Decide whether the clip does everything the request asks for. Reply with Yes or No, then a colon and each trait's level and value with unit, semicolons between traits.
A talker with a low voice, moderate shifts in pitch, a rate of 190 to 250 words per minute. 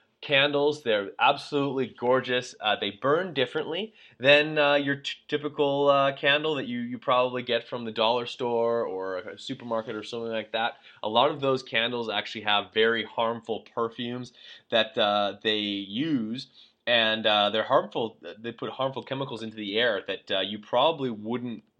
No: low, 120 Hz; average, 3.7 semitones; average, 170 wpm